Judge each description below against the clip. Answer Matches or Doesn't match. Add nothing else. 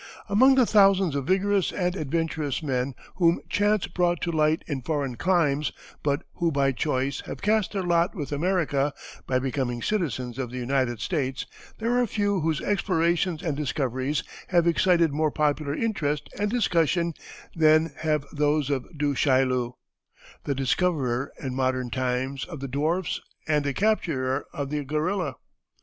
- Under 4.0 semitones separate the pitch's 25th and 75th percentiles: Doesn't match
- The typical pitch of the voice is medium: Matches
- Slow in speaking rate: Doesn't match